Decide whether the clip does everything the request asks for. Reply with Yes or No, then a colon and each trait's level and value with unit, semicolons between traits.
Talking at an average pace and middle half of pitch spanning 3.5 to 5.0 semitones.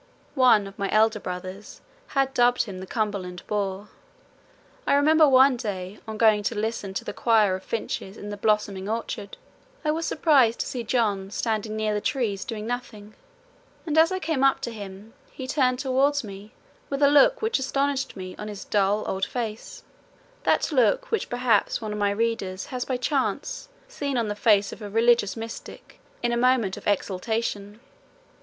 Yes: average, 180 wpm; average, 4.2 semitones